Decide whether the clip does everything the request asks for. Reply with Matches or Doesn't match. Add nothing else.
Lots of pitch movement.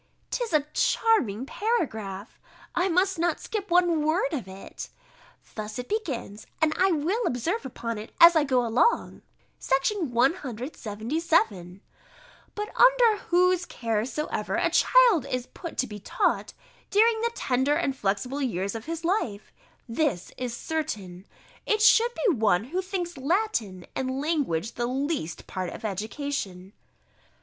Matches